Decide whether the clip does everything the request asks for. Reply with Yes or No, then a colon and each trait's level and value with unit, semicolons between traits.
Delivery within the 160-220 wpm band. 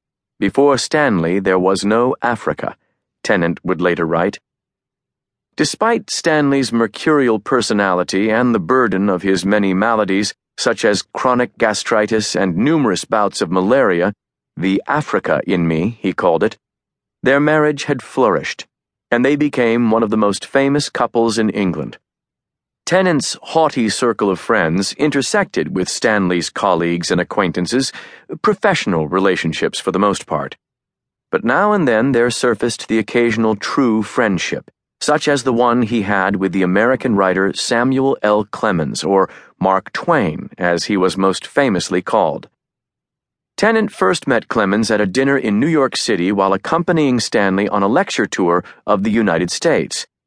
No: average, 145 wpm